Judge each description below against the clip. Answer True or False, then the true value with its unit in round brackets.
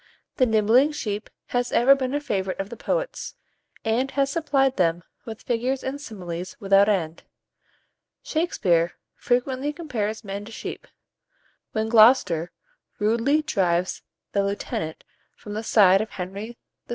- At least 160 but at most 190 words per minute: False (140 wpm)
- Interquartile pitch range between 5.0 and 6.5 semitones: True (5.3 semitones)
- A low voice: False (220 Hz)